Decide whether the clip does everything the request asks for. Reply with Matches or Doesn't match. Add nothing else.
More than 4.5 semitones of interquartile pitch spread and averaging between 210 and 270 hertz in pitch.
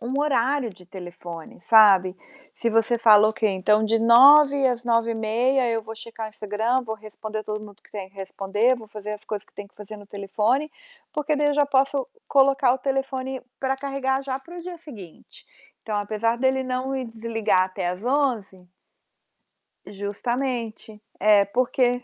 Doesn't match